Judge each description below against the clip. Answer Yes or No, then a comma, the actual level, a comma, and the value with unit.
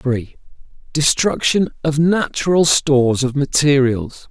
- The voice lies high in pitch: No, medium, 140 Hz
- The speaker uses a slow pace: Yes, slow, 100 wpm